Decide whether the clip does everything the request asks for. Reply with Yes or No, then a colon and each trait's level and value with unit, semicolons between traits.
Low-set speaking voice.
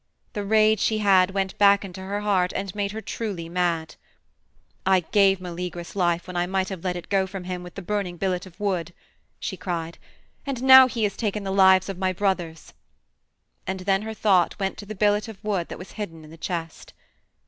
No: high, 190 Hz